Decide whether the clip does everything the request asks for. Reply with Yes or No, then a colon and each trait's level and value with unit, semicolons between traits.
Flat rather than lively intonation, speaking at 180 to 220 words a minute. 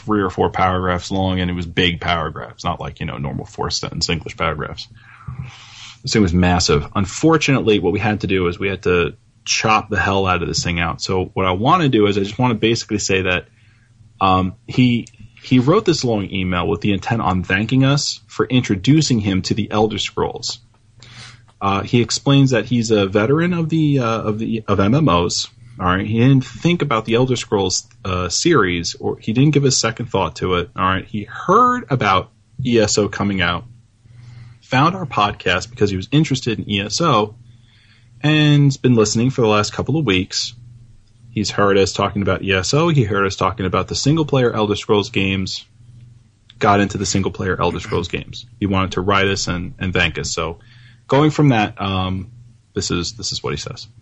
No: average, 3.7 semitones; average, 200 wpm